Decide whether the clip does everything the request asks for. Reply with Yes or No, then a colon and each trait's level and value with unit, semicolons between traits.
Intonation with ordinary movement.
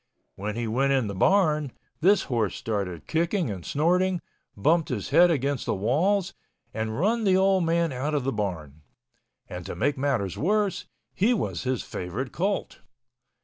No: wide, 8.7 semitones